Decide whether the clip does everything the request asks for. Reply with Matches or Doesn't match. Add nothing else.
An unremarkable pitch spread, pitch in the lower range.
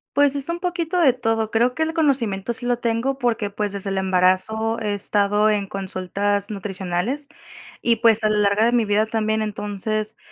Doesn't match